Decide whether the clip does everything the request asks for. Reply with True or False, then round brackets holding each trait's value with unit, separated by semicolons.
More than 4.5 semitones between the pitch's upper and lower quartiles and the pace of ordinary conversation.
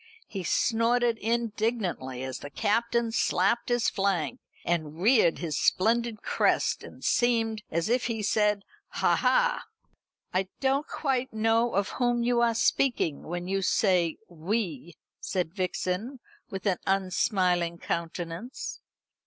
False (5.1 semitones; 130 wpm)